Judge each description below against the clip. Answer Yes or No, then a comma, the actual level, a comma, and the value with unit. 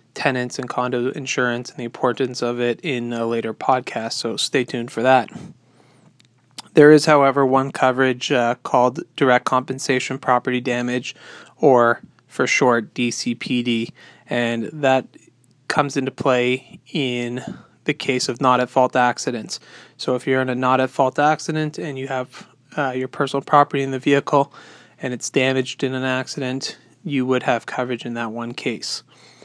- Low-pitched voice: Yes, low, 130 Hz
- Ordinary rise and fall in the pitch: No, narrow, 1.9 semitones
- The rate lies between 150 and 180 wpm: Yes, average, 160 wpm